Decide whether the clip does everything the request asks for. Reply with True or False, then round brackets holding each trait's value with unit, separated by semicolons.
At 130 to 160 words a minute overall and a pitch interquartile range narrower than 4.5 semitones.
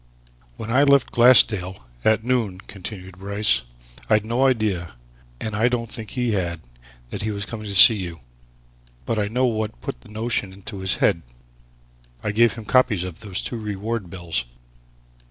False (170 wpm; 3.6 semitones)